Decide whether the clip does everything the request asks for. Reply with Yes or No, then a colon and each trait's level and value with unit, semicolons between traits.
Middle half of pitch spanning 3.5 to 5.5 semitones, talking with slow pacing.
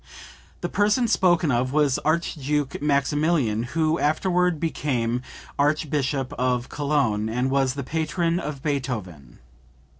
Yes: average, 3.9 semitones; slow, 115 wpm